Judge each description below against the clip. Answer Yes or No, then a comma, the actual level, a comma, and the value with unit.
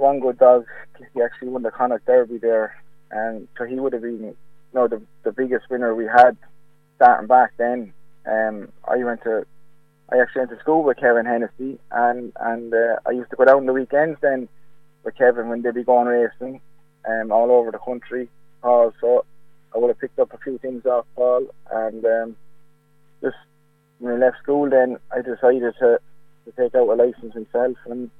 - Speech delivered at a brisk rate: No, average, 195 wpm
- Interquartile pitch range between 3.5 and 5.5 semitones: Yes, average, 4.0 semitones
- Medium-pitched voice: No, low, 125 Hz